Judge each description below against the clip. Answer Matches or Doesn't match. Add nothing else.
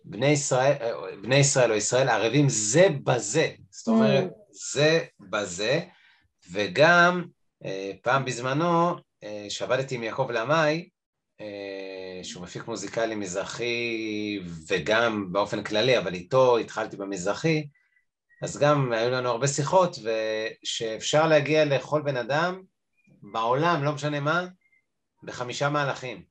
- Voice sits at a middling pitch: Doesn't match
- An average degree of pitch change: Doesn't match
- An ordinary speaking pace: Matches